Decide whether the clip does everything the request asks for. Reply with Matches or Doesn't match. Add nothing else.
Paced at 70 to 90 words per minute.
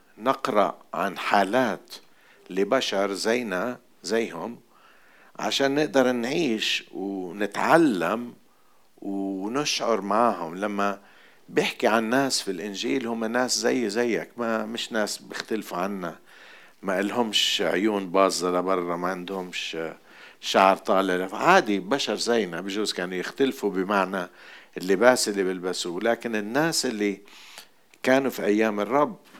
Doesn't match